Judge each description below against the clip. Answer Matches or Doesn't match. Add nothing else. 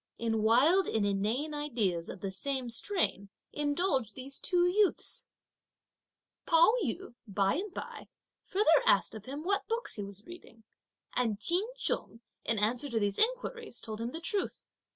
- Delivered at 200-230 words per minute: Doesn't match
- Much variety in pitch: Matches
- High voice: Matches